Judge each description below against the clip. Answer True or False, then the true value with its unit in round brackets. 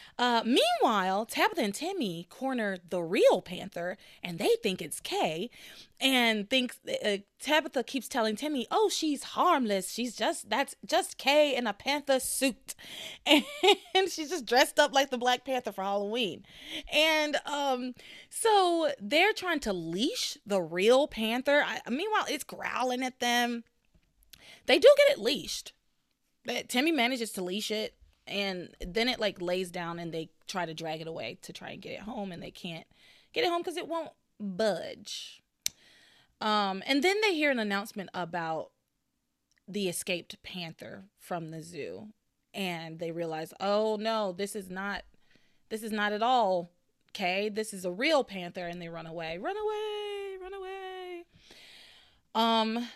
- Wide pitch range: True (7.5 semitones)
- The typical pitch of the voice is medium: False (230 Hz)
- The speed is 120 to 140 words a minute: False (160 wpm)